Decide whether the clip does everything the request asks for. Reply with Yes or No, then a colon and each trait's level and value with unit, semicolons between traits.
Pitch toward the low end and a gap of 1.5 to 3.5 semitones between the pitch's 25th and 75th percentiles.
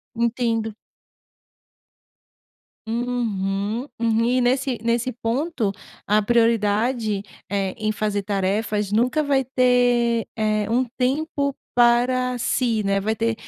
No: high, 230 Hz; average, 2.7 semitones